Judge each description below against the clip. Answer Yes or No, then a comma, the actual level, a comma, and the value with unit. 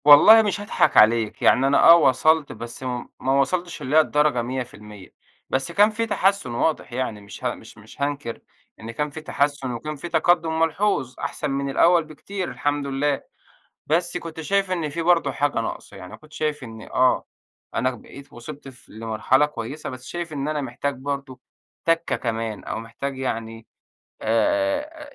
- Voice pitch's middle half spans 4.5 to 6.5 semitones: Yes, average, 5.0 semitones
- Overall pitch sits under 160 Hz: Yes, medium, 140 Hz